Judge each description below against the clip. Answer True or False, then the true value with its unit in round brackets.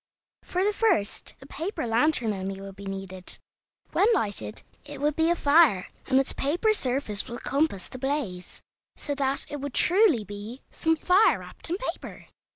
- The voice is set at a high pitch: True (275 Hz)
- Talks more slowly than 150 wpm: False (170 wpm)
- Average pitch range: False (8.0 semitones)